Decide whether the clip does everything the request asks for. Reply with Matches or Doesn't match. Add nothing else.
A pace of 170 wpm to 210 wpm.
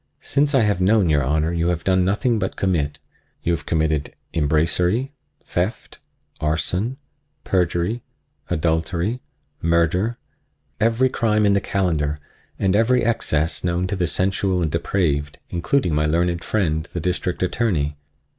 Doesn't match